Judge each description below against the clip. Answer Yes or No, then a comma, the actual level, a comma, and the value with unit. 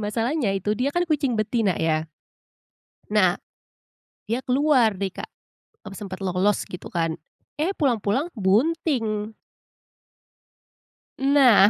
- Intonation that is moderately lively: No, wide, 5.7 semitones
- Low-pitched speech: No, high, 215 Hz